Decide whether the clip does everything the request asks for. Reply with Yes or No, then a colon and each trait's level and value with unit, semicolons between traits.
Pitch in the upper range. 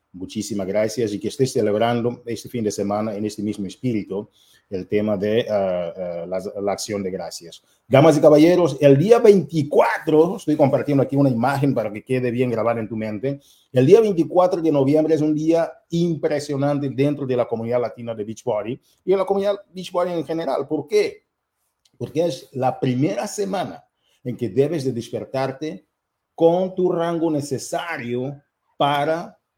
No: low, 135 Hz